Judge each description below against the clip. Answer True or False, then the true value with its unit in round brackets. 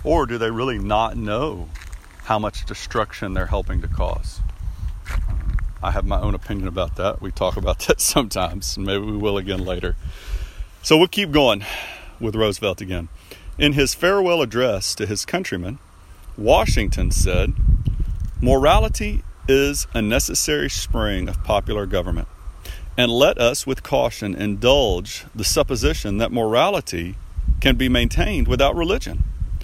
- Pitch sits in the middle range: False (95 Hz)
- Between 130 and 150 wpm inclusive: True (140 wpm)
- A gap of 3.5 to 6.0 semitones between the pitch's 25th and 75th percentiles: True (4.9 semitones)